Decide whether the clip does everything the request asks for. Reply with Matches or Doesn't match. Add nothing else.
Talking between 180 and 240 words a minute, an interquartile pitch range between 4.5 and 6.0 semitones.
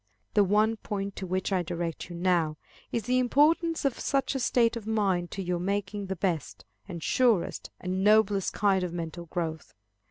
Doesn't match